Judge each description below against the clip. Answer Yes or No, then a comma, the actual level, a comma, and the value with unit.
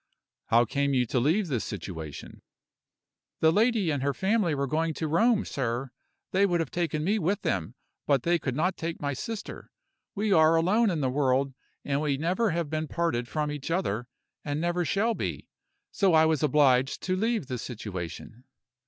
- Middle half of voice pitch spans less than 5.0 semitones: No, average, 5.3 semitones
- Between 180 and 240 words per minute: Yes, average, 185 wpm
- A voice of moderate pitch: Yes, medium, 155 Hz